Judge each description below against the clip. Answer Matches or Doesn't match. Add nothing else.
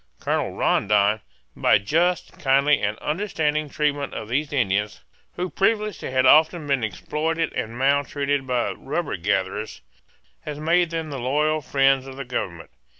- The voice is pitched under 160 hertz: Matches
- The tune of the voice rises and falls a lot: Doesn't match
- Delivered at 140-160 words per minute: Matches